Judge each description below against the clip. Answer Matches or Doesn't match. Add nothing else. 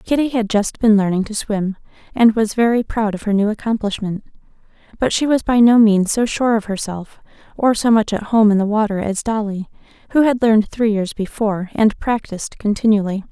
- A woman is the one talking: Matches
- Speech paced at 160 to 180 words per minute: Doesn't match